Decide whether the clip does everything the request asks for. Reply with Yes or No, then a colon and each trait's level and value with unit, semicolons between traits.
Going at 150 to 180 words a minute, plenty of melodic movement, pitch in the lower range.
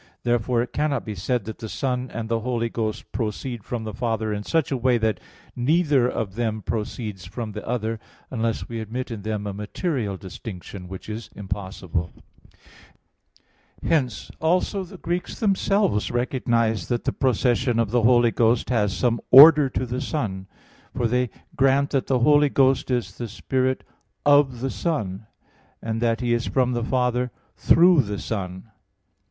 No: average, 170 wpm; average, 3.3 semitones; low, 120 Hz